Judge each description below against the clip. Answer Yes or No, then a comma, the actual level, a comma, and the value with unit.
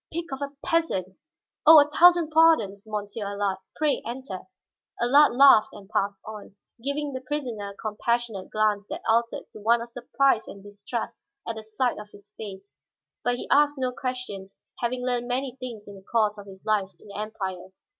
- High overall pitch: Yes, high, 230 Hz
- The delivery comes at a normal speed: Yes, average, 180 wpm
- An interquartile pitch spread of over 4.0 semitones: Yes, average, 4.5 semitones